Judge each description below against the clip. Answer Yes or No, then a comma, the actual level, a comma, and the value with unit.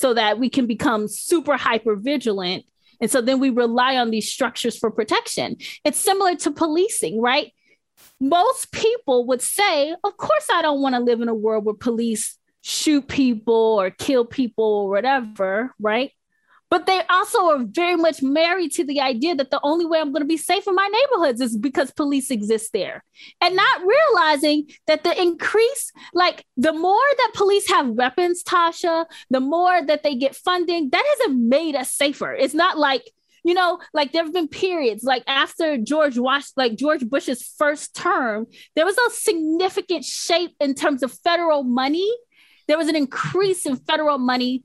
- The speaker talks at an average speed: Yes, average, 180 wpm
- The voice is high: Yes, very high, 300 Hz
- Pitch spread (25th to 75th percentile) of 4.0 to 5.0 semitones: No, wide, 5.4 semitones